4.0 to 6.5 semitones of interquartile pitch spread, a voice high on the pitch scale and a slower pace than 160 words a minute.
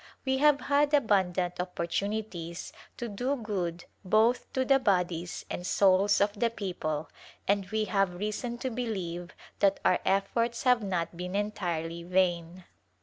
Yes: average, 4.5 semitones; high, 195 Hz; average, 145 wpm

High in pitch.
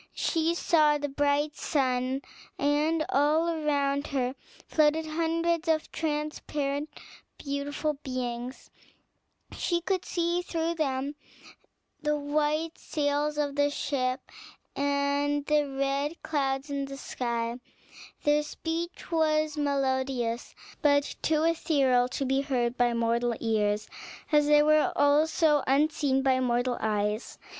Yes: very high, 285 Hz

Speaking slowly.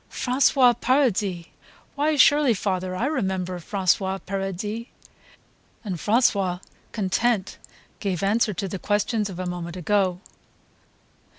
Yes: slow, 110 wpm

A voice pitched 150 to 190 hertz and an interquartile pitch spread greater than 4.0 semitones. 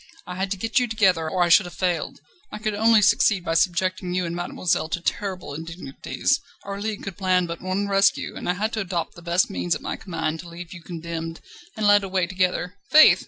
No: medium, 185 Hz; average, 2.8 semitones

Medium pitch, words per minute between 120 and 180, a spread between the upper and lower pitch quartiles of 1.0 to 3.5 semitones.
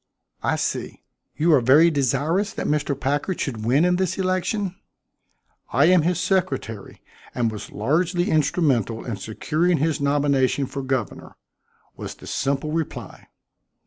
No: medium, 150 Hz; average, 140 wpm; average, 5.0 semitones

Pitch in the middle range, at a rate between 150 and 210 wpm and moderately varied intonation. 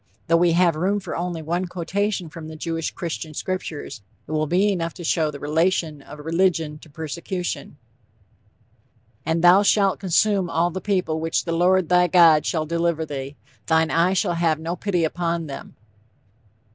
No: medium, 170 Hz; average, 170 wpm; narrow, 2.2 semitones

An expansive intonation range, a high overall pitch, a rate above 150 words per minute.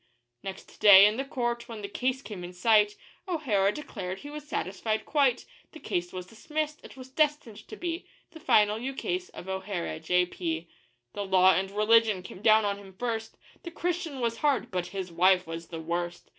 Yes: wide, 6.1 semitones; high, 210 Hz; average, 185 wpm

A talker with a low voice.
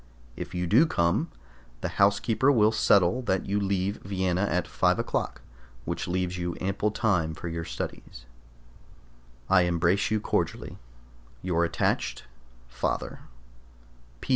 Yes: very low, 95 Hz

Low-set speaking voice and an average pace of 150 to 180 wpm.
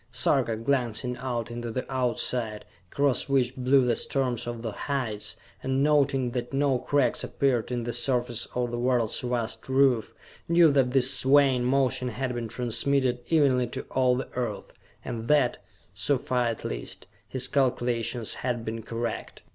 Yes: low, 125 Hz; average, 160 wpm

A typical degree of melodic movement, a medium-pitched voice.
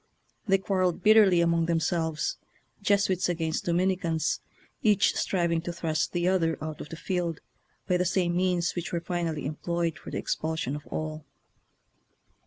No: narrow, 2.1 semitones; medium, 170 Hz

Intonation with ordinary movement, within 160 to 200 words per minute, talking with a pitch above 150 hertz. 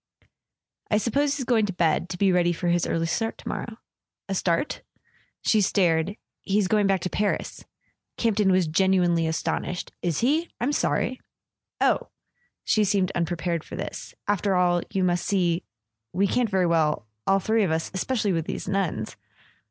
Yes: average, 3.6 semitones; average, 165 wpm; medium, 185 Hz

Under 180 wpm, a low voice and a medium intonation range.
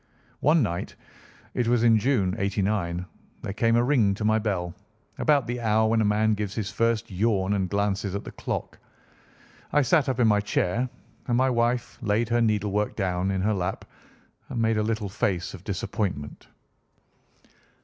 Yes: average, 170 wpm; low, 105 Hz; average, 3.0 semitones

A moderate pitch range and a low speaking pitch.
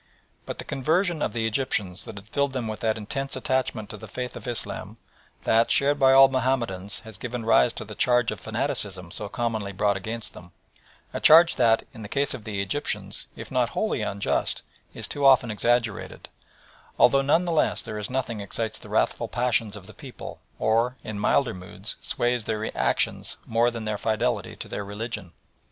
Yes: average, 3.7 semitones; low, 115 Hz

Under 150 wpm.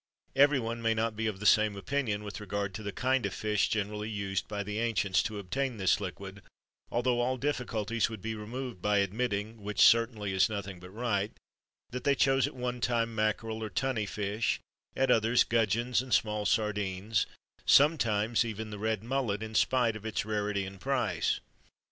No: average, 180 wpm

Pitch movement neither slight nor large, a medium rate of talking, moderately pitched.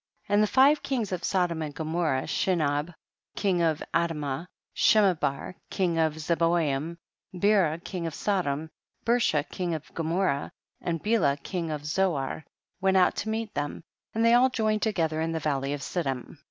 Yes: average, 4.2 semitones; average, 170 wpm; medium, 170 Hz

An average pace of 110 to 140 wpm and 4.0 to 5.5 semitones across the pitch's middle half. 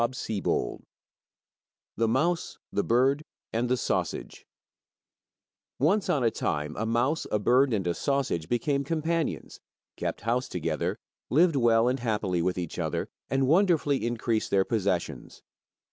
Yes: slow, 135 wpm; average, 4.7 semitones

